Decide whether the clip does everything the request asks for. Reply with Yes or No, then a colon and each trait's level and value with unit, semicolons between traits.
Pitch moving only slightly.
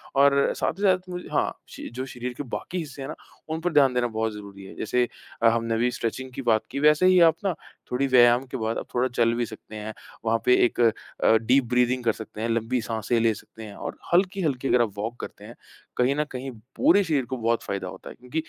No: average, 3.5 semitones